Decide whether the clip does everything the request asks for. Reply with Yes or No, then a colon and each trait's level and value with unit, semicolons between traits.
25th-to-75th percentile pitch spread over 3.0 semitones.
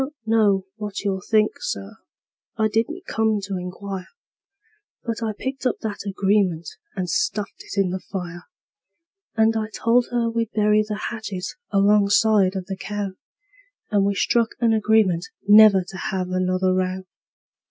No: average, 2.7 semitones